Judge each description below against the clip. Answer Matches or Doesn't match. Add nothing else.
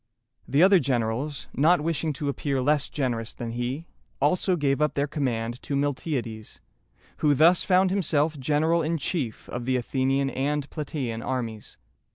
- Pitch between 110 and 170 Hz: Matches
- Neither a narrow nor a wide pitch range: Matches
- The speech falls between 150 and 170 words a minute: Matches